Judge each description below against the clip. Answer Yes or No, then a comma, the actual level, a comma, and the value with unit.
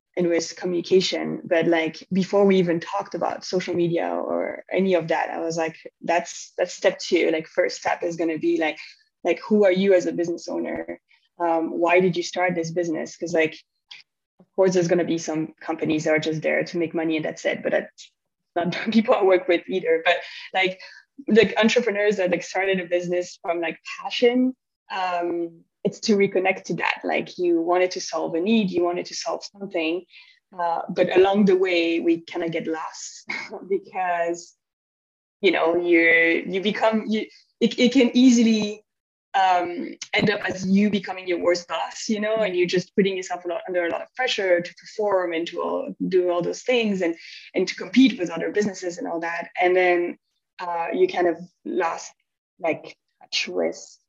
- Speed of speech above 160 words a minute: Yes, average, 200 wpm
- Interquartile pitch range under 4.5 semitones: Yes, average, 3.0 semitones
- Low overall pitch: No, medium, 180 Hz